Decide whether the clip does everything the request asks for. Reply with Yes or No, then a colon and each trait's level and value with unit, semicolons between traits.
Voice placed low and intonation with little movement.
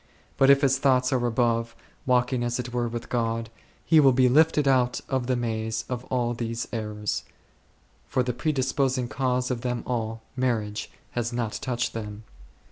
Yes: low, 120 Hz; narrow, 2.0 semitones